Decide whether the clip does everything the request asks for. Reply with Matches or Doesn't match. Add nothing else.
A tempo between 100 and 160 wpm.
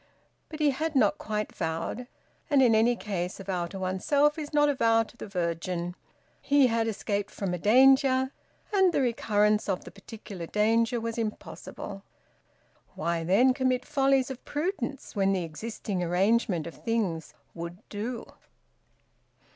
Matches